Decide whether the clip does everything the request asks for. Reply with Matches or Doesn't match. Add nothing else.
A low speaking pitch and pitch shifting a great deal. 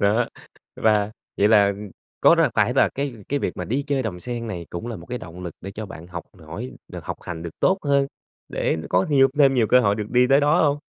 Matches